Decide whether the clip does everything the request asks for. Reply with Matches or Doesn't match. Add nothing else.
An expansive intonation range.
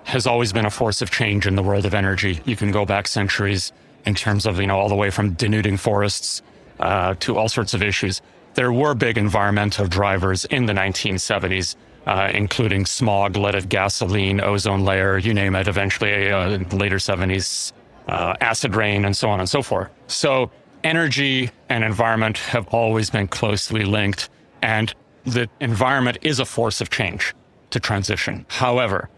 Doesn't match